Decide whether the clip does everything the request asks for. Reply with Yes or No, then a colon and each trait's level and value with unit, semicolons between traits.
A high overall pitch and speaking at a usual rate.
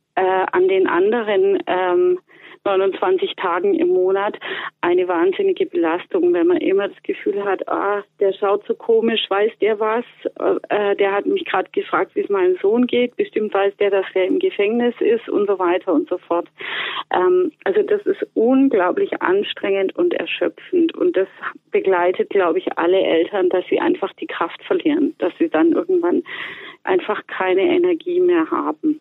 Yes: very high, 345 Hz; average, 165 wpm